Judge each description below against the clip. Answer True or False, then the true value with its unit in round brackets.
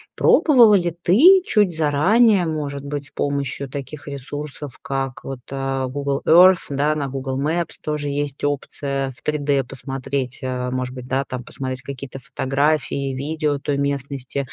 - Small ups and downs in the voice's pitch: True (2.1 semitones)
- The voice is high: False (140 Hz)